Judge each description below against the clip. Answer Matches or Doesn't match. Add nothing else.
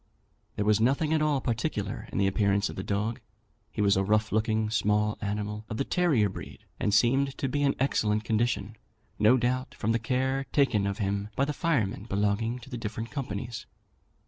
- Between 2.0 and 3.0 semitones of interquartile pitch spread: Doesn't match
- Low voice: Matches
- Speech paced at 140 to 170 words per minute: Doesn't match